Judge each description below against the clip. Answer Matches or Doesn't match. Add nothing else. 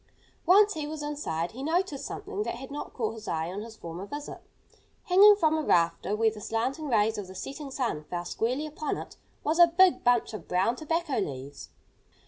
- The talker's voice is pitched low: Doesn't match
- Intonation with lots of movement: Matches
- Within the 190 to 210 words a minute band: Matches